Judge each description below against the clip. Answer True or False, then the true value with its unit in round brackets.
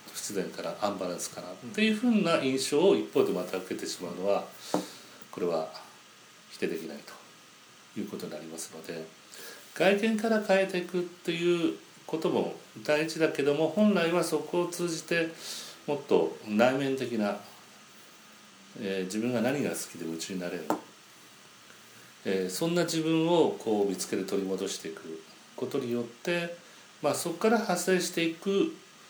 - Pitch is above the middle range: False (160 Hz)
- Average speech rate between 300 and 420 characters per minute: True (310 characters per minute)